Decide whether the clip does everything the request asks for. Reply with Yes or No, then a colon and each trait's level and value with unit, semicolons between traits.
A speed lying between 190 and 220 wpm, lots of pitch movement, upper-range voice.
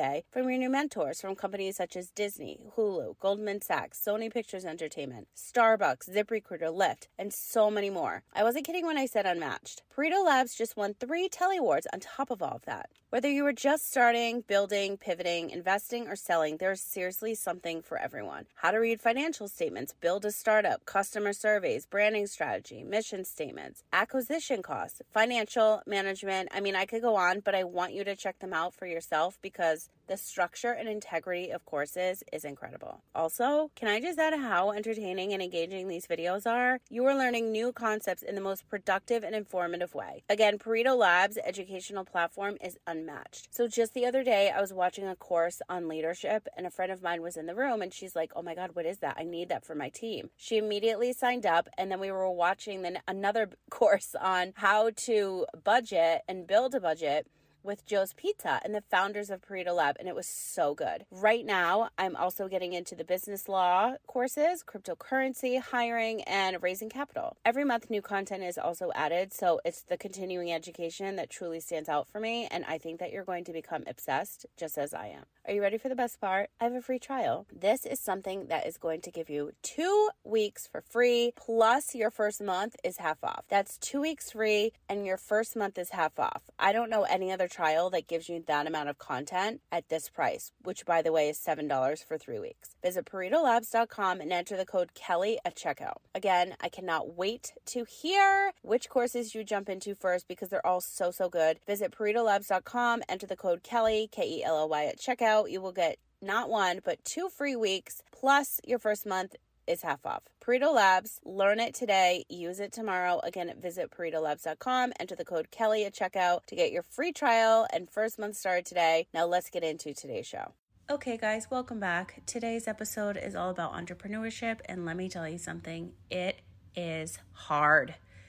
No: average, 200 wpm; average, 4.5 semitones; high, 200 Hz